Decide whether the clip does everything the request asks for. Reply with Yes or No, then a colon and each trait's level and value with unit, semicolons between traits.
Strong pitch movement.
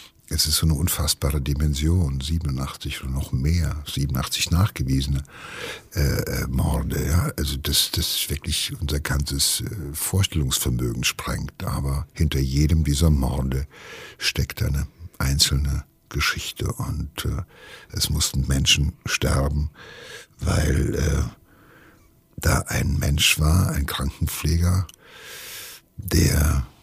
No: average, 3.2 semitones